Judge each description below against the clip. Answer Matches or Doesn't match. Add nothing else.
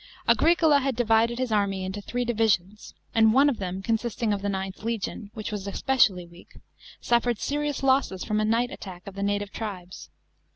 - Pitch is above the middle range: Matches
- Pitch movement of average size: Matches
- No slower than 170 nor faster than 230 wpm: Matches